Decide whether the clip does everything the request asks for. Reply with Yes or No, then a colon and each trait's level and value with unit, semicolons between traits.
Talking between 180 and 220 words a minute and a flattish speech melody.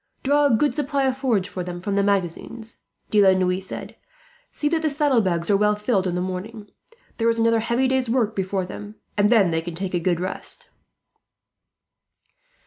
No: average, 195 wpm; average, 4.7 semitones